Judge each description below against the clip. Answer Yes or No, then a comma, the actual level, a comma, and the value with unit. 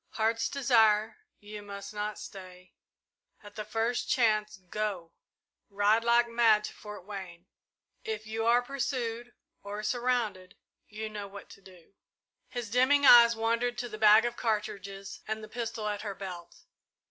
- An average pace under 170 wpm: Yes, average, 155 wpm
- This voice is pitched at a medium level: No, high, 215 Hz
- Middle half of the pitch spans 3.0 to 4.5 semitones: No, narrow, 2.4 semitones